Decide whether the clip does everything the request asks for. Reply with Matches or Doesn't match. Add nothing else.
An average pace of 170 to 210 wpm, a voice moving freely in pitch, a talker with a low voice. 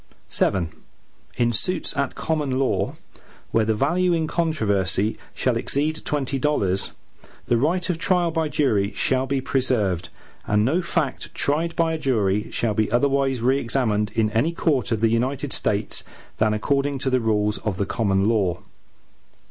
Doesn't match